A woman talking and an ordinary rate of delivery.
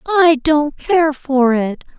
Yes: female; average, 150 wpm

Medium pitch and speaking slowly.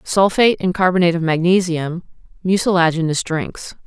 Yes: medium, 175 Hz; slow, 110 wpm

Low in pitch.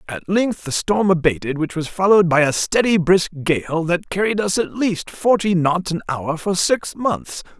No: medium, 180 Hz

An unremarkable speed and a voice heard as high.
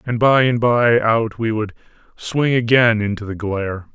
No: average, 185 wpm; low, 115 Hz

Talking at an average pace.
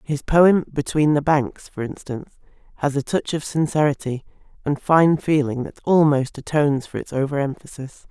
Yes: average, 165 wpm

